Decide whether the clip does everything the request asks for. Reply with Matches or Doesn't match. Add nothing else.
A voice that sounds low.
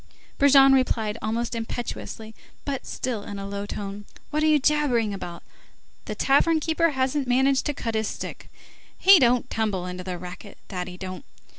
Doesn't match